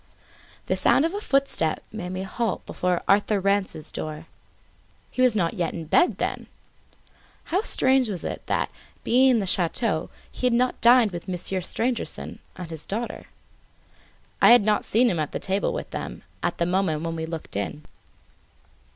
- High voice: Yes, high, 195 Hz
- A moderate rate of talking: Yes, average, 170 wpm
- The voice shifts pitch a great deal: Yes, wide, 6.0 semitones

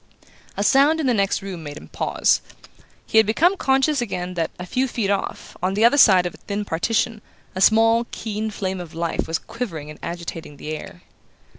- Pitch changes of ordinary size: Yes, average, 4.9 semitones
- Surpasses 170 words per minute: Yes, average, 200 wpm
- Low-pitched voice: No, high, 200 Hz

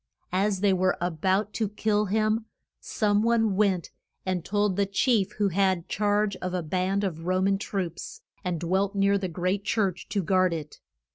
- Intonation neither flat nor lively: No, narrow, 2.1 semitones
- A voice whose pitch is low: No, high, 195 Hz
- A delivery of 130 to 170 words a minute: No, average, 185 wpm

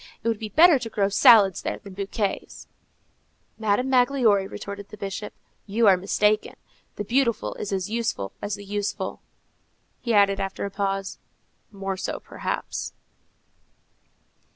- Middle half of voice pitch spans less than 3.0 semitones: Yes, narrow, 2.5 semitones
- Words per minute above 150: No, average, 140 wpm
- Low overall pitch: No, high, 205 Hz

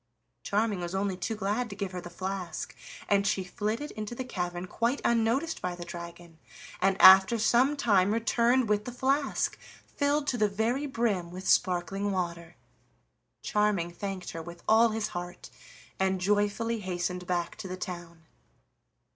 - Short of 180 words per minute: Yes, average, 160 wpm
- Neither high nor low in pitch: No, high, 200 Hz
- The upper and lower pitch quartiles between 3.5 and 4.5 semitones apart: Yes, average, 4.2 semitones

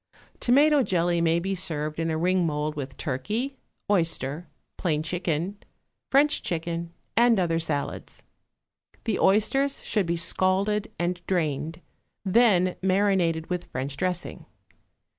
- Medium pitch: Yes, medium, 175 Hz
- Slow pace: Yes, slow, 120 wpm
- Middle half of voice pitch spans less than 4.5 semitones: Yes, average, 3.7 semitones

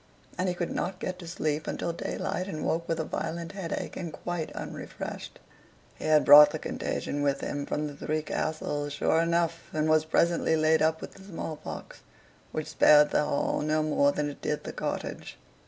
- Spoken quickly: No, average, 190 wpm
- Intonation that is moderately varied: No, narrow, 2.1 semitones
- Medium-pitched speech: Yes, medium, 155 Hz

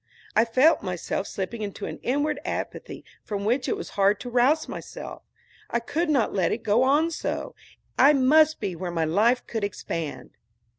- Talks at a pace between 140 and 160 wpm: No, average, 180 wpm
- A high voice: Yes, high, 235 Hz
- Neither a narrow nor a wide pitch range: No, wide, 6.4 semitones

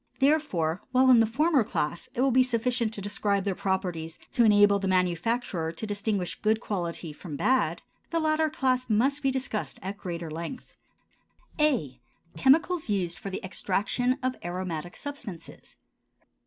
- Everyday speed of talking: Yes, average, 155 wpm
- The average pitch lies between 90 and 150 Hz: No, high, 210 Hz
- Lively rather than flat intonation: Yes, wide, 6.1 semitones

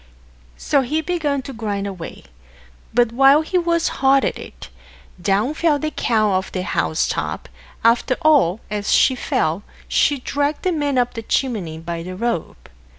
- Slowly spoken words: No, average, 170 wpm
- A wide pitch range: Yes, wide, 6.5 semitones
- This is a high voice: Yes, high, 245 Hz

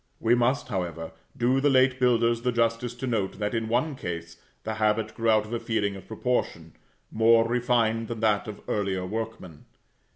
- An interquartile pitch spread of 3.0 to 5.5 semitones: No, narrow, 2.5 semitones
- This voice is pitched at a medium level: No, low, 115 Hz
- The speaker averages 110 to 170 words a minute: No, average, 185 wpm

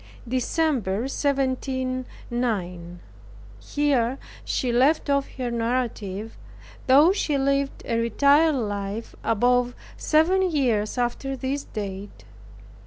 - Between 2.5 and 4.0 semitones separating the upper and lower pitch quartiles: Yes, average, 3.6 semitones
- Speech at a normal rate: No, slow, 95 wpm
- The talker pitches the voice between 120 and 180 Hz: No, very high, 255 Hz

